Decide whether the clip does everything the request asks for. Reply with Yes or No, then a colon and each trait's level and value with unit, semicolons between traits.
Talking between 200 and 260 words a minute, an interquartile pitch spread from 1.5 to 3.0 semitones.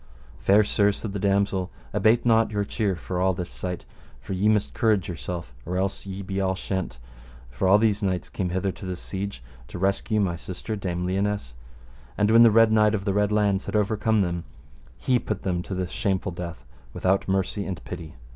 Yes: fast, 205 wpm; narrow, 2.4 semitones